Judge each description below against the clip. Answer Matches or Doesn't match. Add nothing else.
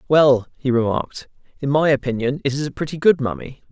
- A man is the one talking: Matches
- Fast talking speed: Doesn't match